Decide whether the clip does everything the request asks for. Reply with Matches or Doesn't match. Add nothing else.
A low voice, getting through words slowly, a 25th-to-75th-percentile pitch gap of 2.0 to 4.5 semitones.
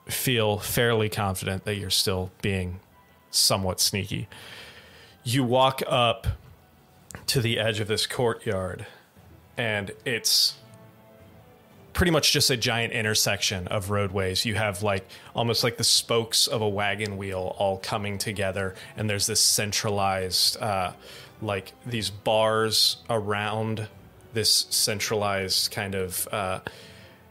Matches